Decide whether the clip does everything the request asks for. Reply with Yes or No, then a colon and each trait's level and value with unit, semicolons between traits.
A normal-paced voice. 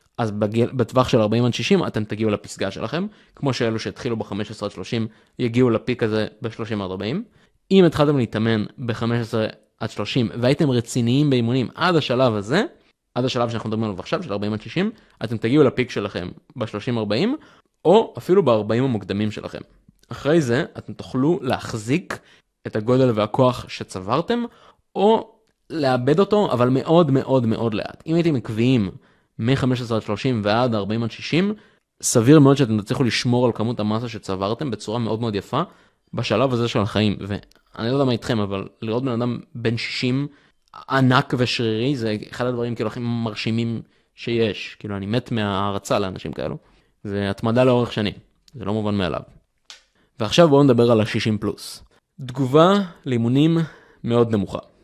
No: fast, 155 wpm